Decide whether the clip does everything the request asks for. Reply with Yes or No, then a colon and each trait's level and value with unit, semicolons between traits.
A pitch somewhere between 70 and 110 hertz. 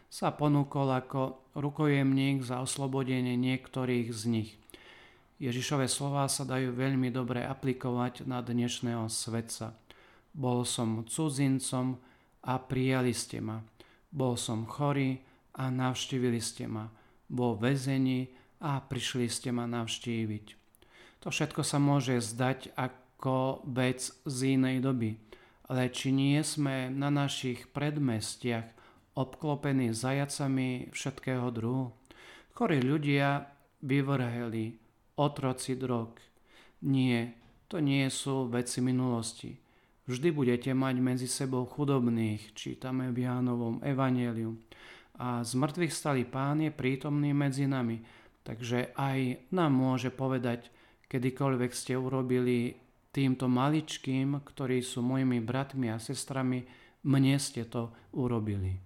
No: low, 130 Hz